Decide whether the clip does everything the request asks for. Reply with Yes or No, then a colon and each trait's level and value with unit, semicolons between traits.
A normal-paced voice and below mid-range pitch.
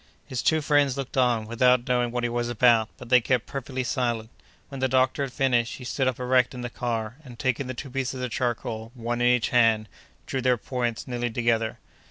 No: fast, 220 wpm; low, 125 Hz